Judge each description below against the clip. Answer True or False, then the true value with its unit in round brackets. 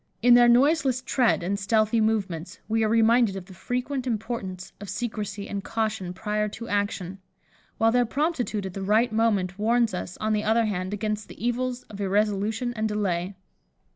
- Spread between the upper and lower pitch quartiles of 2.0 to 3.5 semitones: True (3.0 semitones)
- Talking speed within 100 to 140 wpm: False (175 wpm)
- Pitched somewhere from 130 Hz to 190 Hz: False (215 Hz)